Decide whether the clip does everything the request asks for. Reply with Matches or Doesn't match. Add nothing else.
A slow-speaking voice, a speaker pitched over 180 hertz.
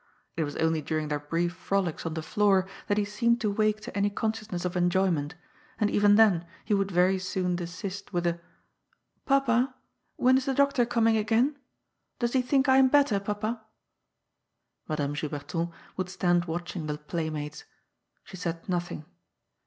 Doesn't match